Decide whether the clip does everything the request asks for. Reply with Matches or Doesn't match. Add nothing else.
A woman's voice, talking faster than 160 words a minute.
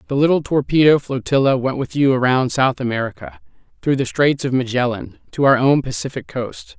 Doesn't match